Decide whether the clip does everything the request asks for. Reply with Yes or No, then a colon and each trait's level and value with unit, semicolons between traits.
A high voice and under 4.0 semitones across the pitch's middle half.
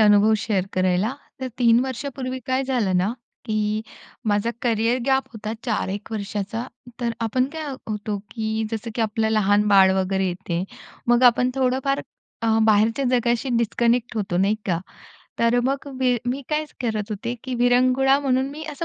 Yes: high, 230 Hz; average, 3.5 semitones